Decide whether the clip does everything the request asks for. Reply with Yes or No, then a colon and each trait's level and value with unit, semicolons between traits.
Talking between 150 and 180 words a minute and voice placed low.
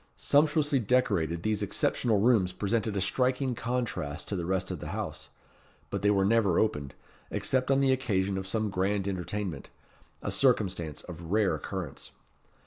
Yes: average, 155 wpm; low, 100 Hz